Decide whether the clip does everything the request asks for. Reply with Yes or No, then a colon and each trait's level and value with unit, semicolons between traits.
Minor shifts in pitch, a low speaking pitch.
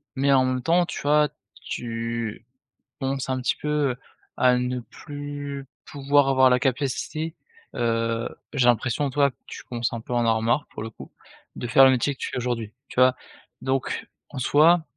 No: average, 3.0 semitones; low, 130 Hz